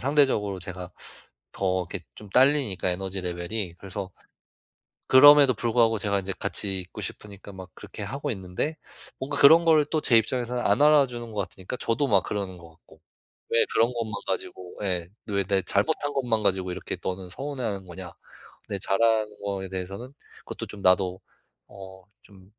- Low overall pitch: Yes, low, 100 Hz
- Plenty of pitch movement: No, average, 4.7 semitones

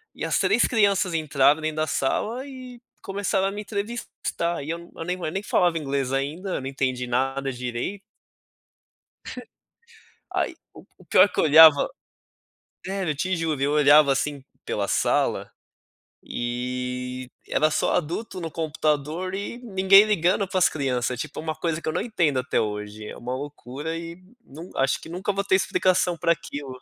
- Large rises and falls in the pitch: Yes, wide, 5.7 semitones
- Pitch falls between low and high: Yes, medium, 155 Hz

